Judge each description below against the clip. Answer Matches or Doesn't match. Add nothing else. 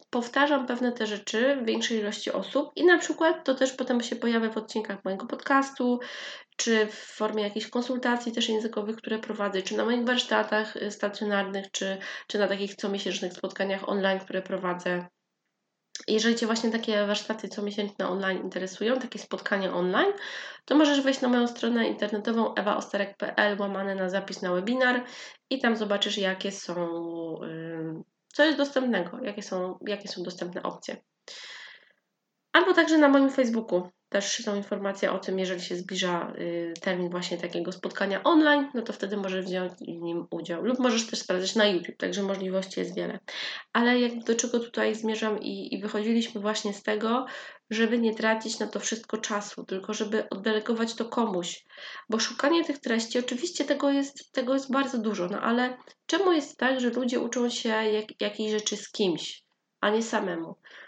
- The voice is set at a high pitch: Matches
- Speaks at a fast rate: Matches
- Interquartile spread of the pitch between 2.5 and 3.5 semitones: Doesn't match